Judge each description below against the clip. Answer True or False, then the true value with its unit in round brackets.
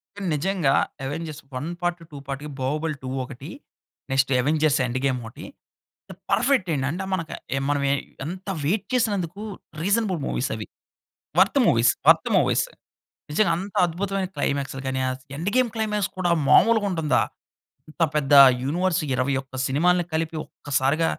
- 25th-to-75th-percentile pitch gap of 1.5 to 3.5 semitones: False (5.3 semitones)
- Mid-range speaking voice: True (160 Hz)